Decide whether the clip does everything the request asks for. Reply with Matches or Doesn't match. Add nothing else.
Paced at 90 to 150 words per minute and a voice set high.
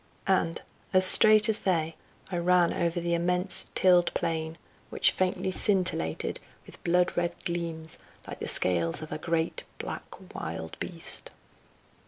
Doesn't match